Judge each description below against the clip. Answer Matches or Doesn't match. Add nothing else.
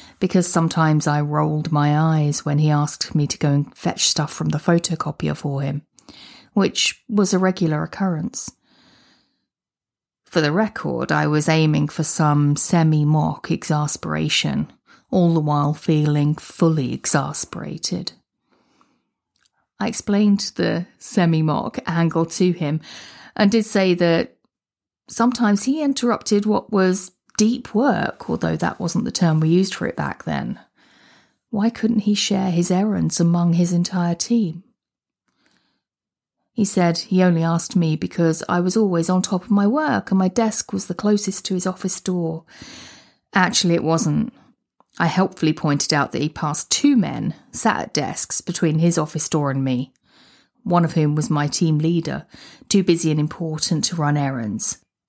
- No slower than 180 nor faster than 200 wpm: Doesn't match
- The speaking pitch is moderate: Matches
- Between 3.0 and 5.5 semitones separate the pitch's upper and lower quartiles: Matches